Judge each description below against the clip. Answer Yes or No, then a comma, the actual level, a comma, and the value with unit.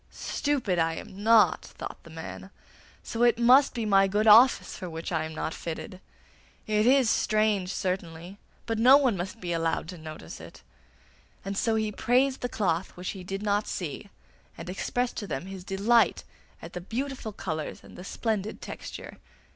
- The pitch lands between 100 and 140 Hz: No, high, 200 Hz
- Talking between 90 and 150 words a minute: No, average, 180 wpm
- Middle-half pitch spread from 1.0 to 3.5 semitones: No, average, 4.1 semitones